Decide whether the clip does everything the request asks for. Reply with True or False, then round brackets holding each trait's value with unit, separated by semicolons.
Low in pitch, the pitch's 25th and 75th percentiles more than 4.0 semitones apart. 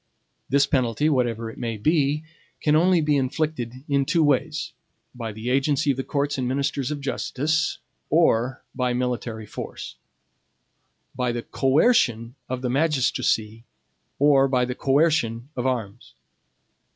False (130 Hz; 3.4 semitones)